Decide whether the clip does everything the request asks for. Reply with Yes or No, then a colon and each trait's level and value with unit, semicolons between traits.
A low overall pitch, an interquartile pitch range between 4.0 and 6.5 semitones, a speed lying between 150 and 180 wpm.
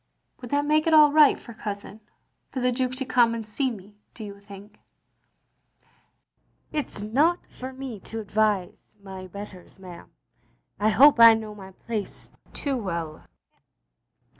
No: high, 220 Hz; average, 4.5 semitones; average, 165 wpm